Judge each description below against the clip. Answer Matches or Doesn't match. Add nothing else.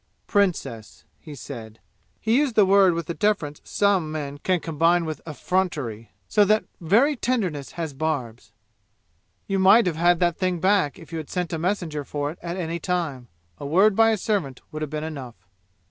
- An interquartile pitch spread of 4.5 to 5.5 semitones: Matches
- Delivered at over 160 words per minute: Matches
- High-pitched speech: Doesn't match